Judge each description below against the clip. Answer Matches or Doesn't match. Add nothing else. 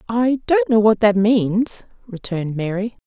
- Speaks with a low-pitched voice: Doesn't match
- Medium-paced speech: Matches